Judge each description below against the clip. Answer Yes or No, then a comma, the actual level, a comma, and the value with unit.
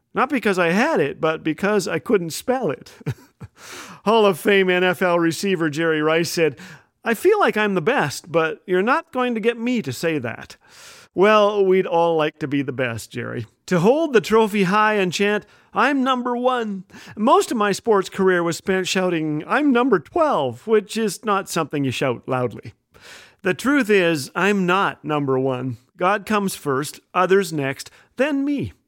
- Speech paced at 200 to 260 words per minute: No, average, 180 wpm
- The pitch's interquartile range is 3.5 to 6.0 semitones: Yes, wide, 5.4 semitones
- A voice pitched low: No, high, 190 Hz